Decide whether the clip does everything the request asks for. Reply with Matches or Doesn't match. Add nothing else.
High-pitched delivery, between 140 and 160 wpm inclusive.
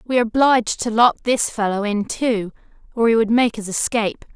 Doesn't match